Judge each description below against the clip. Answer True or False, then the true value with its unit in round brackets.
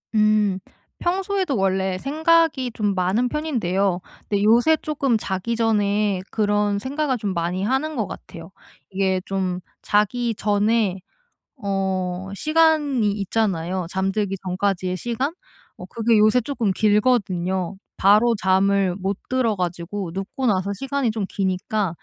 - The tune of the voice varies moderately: True (4.0 semitones)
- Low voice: False (205 Hz)